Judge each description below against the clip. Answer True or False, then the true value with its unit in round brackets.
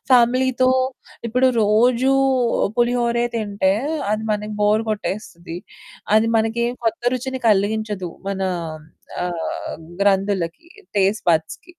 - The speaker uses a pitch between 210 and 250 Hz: True (215 Hz)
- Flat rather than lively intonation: False (3.2 semitones)